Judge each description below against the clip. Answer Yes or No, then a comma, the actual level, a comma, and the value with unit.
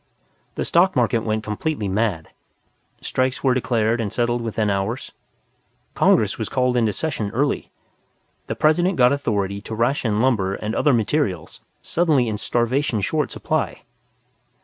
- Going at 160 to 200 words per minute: No, average, 140 wpm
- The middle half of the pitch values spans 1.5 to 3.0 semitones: No, average, 3.8 semitones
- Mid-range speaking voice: No, low, 120 Hz